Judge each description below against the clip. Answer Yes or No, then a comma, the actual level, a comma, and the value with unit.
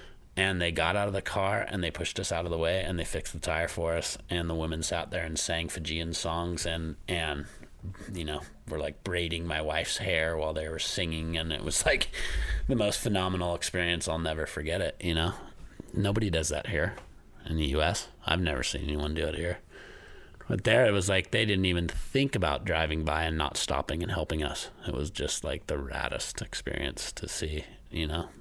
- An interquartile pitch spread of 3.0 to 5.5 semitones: No, narrow, 2.4 semitones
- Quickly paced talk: Yes, fast, 215 wpm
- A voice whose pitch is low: Yes, very low, 85 Hz